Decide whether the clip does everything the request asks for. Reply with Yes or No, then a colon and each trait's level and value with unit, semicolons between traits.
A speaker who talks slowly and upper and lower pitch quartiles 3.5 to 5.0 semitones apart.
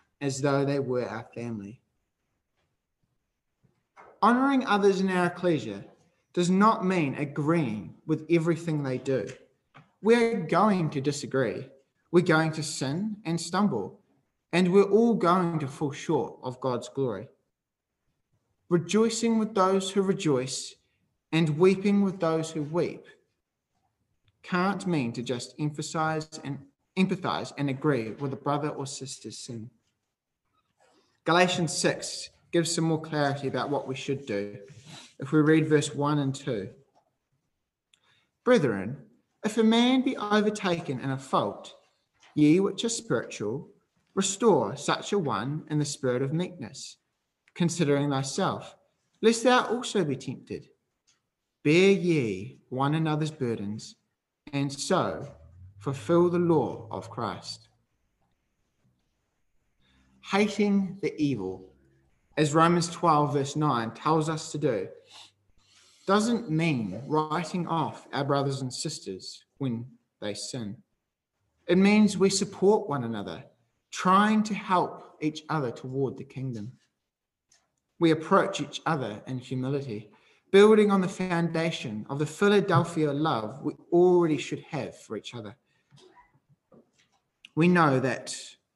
No: slow, 125 wpm; wide, 5.5 semitones